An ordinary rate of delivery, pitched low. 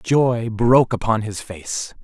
Yes: average, 150 wpm; low, 115 Hz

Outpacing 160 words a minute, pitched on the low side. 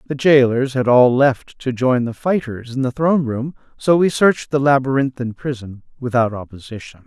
Yes: average, 180 wpm; low, 130 Hz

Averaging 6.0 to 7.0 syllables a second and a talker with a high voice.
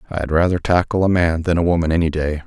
No: 6.3 syllables/s; very low, 85 Hz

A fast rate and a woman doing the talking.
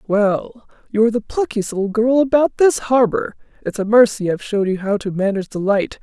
Yes: fast, 210 wpm; female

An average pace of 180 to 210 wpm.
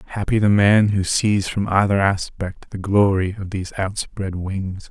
No: average, 170 wpm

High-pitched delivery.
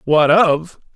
No: medium, 165 Hz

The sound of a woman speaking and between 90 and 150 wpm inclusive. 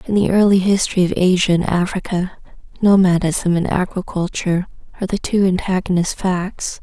Yes: female; average, 140 wpm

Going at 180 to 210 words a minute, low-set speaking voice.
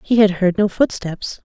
No: average, 200 wpm; high, 200 Hz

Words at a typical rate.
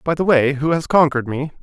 No: fast, 260 wpm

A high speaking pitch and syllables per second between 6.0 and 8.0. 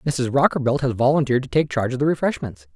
No: low, 135 Hz; 7.0 syllables/s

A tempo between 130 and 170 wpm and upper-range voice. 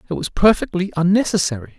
No: slow, 135 wpm; medium, 170 Hz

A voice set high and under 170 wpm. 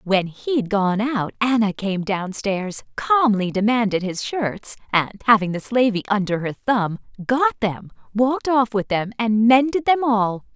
Yes: high, 220 Hz; average, 160 wpm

